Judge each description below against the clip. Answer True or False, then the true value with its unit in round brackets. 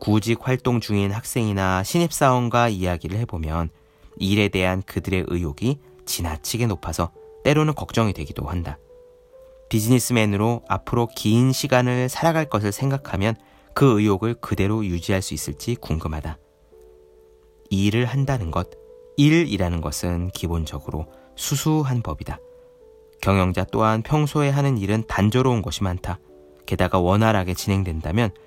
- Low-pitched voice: True (105 Hz)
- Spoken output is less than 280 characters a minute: False (310 characters per minute)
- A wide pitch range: True (6.1 semitones)